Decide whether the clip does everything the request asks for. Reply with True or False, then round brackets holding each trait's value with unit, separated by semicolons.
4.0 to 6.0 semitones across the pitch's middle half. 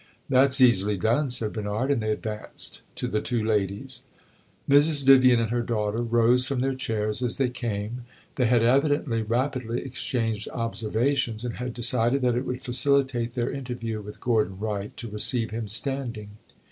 False (2.8 semitones)